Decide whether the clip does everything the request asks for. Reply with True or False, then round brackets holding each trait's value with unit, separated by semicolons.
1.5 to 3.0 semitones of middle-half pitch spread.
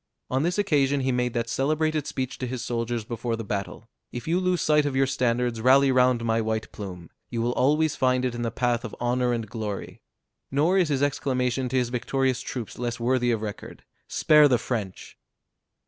True (2.7 semitones)